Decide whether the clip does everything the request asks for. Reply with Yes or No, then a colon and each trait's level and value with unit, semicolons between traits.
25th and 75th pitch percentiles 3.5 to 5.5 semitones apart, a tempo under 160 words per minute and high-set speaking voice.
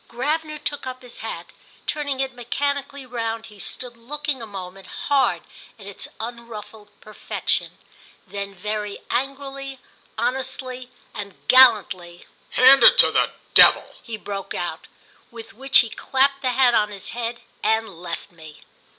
Yes: average, 4.3 semitones; average, 140 wpm; high, 235 Hz